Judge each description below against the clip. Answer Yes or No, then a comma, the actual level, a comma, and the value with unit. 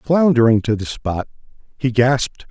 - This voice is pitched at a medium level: No, low, 125 Hz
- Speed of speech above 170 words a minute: No, average, 145 wpm